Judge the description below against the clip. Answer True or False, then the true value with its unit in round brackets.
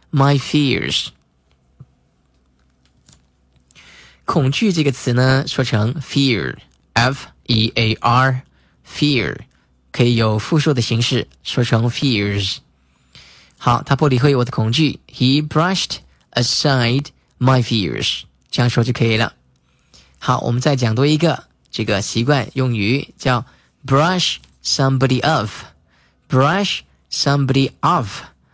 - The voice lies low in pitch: True (120 Hz)